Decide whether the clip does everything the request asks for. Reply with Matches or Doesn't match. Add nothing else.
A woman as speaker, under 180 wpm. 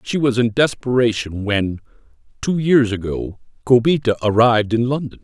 Doesn't match